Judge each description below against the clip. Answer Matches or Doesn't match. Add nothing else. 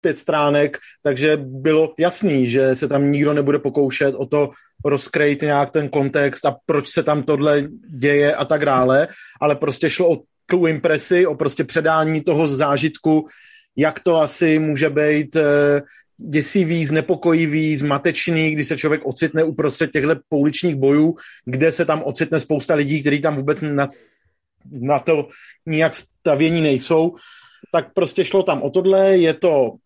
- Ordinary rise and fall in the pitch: Doesn't match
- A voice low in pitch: Doesn't match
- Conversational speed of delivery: Matches